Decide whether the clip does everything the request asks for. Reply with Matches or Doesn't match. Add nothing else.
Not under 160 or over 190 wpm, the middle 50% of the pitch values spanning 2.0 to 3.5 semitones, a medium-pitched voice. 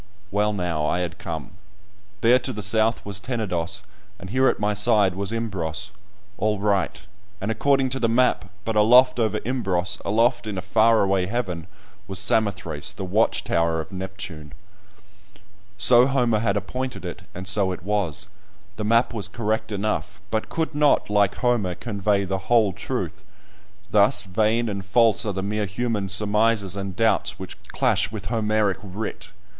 Doesn't match